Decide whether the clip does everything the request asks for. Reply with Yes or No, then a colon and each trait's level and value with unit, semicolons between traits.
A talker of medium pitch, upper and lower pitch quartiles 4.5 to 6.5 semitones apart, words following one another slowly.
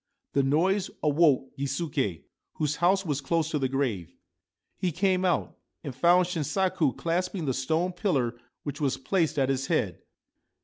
No: medium, 150 Hz; average, 4.8 semitones; average, 150 wpm